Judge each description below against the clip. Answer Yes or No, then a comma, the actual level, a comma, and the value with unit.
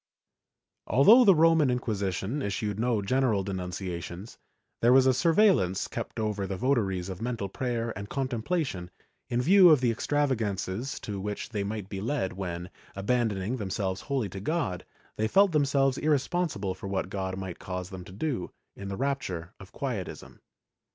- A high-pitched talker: No, low, 110 Hz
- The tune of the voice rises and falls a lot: Yes, wide, 5.8 semitones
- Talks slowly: No, average, 165 wpm